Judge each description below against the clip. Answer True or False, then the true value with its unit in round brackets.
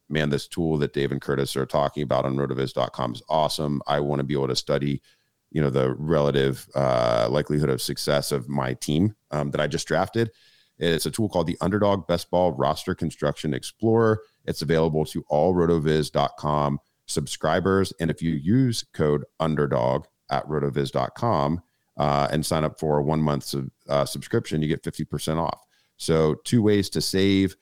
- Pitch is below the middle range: True (75 Hz)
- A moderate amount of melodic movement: True (3.1 semitones)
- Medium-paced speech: True (180 wpm)